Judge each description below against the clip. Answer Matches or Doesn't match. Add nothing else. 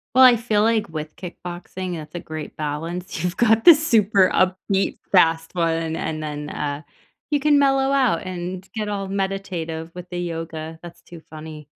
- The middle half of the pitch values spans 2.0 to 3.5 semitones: Doesn't match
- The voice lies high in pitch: Doesn't match